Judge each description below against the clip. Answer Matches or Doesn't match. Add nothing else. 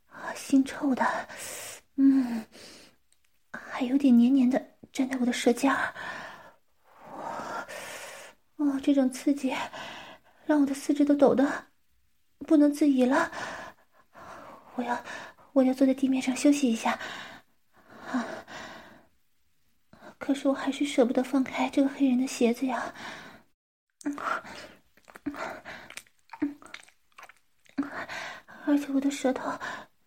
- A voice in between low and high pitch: Doesn't match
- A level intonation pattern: Matches